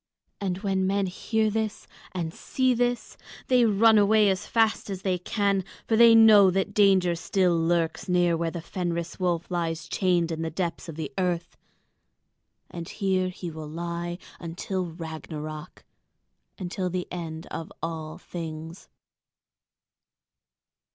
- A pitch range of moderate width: Yes, average, 3.1 semitones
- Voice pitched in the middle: Yes, medium, 180 Hz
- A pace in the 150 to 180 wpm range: No, average, 140 wpm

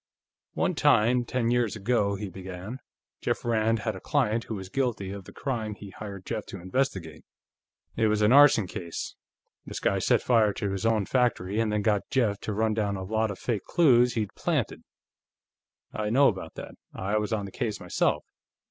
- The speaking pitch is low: Yes, low, 110 Hz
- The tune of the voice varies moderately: Yes, average, 3.0 semitones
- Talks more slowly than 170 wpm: No, average, 190 wpm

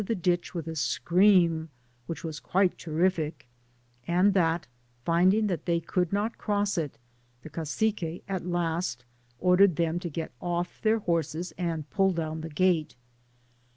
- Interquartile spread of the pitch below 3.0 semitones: Yes, narrow, 2.5 semitones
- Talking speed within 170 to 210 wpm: No, average, 145 wpm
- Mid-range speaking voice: Yes, medium, 175 Hz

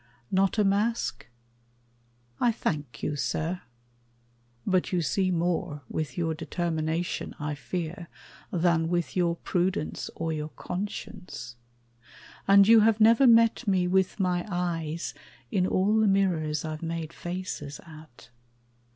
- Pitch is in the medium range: Yes, medium, 175 Hz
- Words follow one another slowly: Yes, slow, 125 wpm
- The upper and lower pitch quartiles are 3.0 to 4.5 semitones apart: Yes, average, 3.4 semitones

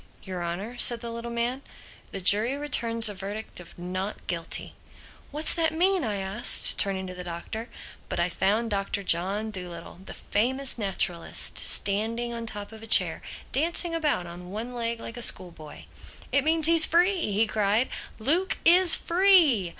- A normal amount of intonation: No, wide, 6.1 semitones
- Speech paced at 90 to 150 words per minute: No, average, 165 wpm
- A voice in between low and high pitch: No, high, 220 Hz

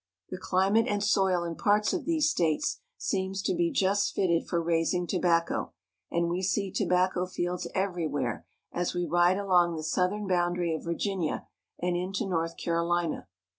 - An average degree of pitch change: No, narrow, 2.2 semitones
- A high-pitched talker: No, medium, 180 Hz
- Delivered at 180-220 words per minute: No, average, 170 wpm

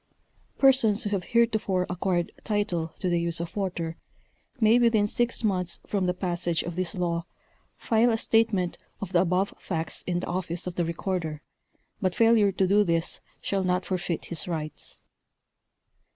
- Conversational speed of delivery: Yes, average, 165 wpm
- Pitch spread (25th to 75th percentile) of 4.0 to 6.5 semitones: No, average, 3.2 semitones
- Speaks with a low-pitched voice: No, medium, 185 Hz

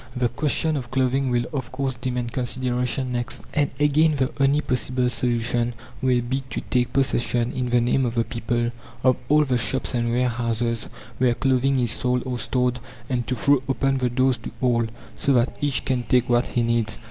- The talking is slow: No, average, 195 wpm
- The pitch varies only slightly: Yes, narrow, 1.7 semitones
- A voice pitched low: Yes, low, 125 Hz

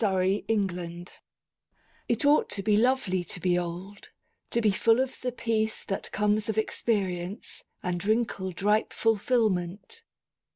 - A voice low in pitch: No, high, 205 Hz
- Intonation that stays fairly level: No, average, 3.5 semitones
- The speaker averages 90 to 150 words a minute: Yes, slow, 135 wpm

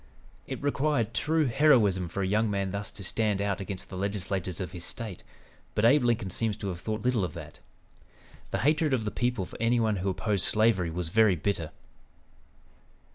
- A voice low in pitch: Yes, low, 105 Hz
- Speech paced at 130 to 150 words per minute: No, average, 190 wpm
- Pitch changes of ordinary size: Yes, average, 3.7 semitones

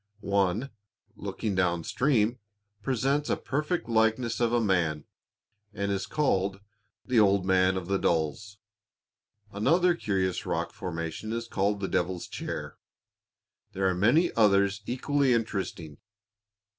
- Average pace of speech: No, slow, 125 wpm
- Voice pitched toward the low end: Yes, low, 100 Hz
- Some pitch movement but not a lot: Yes, average, 4.2 semitones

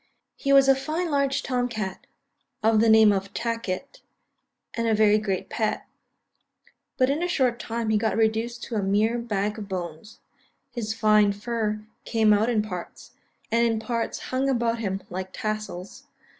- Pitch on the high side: Yes, high, 220 Hz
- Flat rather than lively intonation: Yes, narrow, 2.2 semitones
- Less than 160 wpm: No, average, 170 wpm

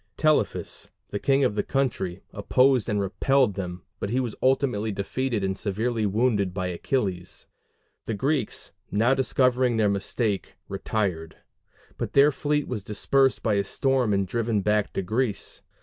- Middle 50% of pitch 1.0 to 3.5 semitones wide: No, average, 4.7 semitones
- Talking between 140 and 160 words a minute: Yes, average, 150 wpm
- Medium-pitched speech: No, low, 110 Hz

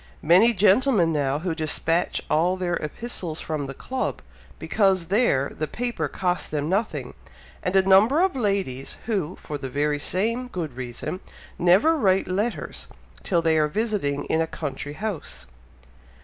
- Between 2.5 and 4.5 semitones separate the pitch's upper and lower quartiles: No, wide, 5.6 semitones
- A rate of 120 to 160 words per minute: Yes, average, 150 wpm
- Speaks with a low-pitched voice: No, medium, 180 Hz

